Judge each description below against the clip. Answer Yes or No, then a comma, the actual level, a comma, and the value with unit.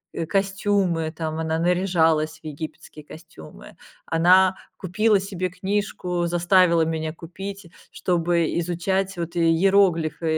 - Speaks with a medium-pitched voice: Yes, medium, 175 Hz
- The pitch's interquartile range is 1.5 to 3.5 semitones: Yes, average, 2.8 semitones